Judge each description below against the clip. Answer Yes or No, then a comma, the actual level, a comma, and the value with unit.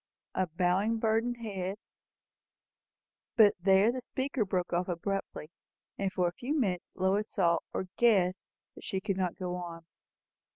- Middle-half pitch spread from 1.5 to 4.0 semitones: Yes, average, 3.4 semitones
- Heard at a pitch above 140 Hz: Yes, high, 190 Hz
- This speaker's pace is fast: No, average, 155 wpm